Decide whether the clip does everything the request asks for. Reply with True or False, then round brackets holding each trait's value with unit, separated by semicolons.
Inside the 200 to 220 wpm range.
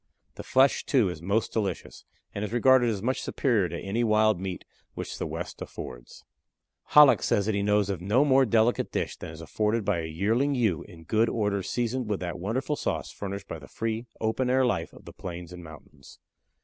True (205 wpm)